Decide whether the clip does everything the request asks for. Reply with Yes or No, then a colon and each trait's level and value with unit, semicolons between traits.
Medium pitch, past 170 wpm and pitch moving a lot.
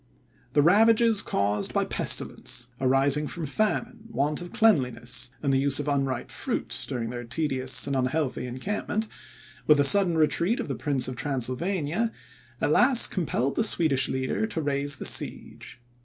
No: medium, 145 Hz; average, 155 wpm; wide, 6.0 semitones